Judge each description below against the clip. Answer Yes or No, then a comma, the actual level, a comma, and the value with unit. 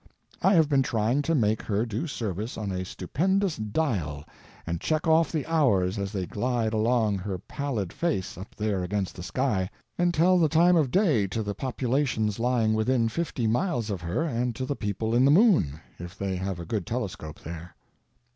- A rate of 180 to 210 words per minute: Yes, average, 195 wpm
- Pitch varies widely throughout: Yes, wide, 6.7 semitones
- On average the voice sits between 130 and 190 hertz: No, low, 115 Hz